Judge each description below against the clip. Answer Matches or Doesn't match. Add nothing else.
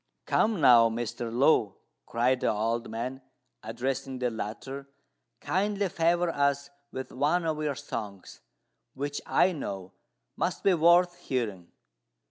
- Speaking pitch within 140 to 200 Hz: Doesn't match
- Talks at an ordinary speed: Doesn't match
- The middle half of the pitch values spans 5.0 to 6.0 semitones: Matches